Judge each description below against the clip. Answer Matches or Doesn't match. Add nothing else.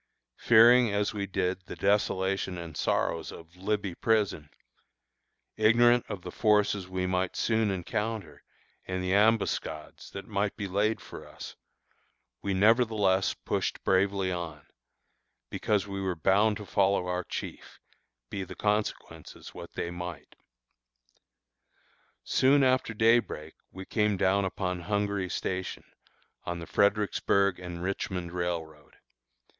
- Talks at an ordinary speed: Doesn't match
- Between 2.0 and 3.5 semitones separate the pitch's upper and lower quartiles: Matches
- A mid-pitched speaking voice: Doesn't match